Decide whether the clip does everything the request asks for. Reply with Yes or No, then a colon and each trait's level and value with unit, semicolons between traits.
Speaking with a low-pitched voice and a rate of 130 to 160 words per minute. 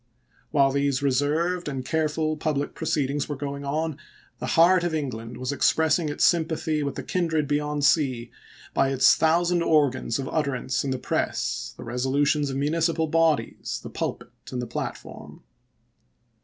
No: medium, 145 Hz; average, 155 wpm